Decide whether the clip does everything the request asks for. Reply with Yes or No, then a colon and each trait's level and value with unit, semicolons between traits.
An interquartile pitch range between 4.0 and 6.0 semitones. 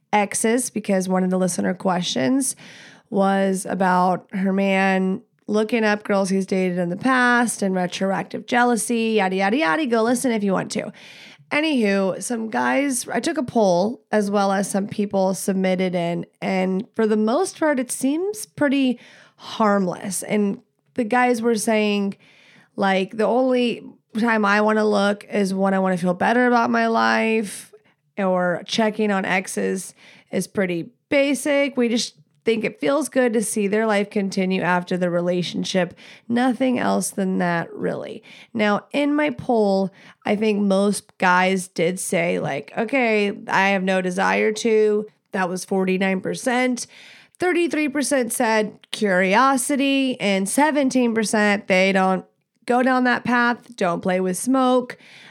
Yes: average, 4.3 semitones